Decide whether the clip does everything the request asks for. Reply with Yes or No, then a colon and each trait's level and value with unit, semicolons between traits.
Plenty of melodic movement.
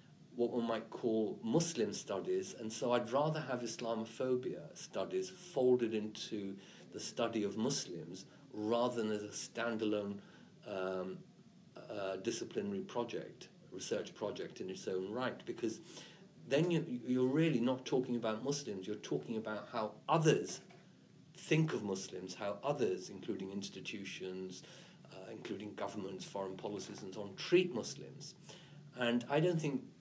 Yes: wide, 6.0 semitones